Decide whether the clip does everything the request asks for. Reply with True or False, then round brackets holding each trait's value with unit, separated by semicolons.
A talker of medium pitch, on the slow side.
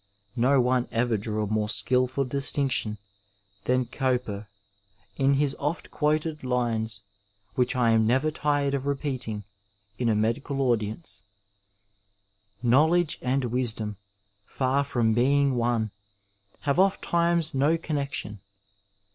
False (130 Hz; 120 wpm)